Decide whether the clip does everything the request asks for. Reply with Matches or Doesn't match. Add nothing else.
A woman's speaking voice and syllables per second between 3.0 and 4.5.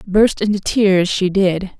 Matches